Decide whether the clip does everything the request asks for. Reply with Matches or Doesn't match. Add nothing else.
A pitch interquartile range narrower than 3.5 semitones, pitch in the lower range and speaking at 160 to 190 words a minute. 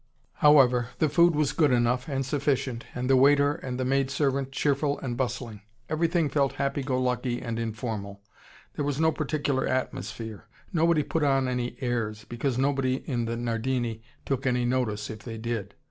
Matches